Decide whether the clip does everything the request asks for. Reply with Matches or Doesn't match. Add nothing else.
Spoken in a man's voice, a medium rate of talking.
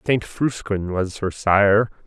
Matches